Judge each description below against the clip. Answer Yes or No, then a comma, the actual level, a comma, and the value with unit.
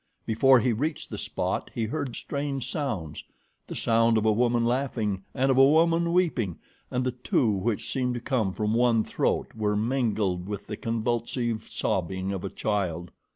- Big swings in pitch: No, average, 3.8 semitones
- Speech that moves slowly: No, average, 175 wpm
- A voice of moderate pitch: No, low, 115 Hz